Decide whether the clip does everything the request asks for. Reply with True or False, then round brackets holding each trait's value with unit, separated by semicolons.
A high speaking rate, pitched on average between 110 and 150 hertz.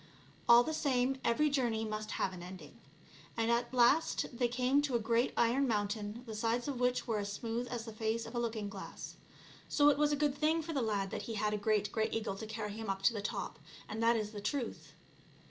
False (235 wpm; 230 Hz)